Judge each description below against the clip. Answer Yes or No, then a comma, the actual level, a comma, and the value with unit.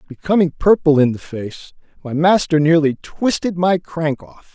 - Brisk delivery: No, average, 160 wpm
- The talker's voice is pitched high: No, medium, 160 Hz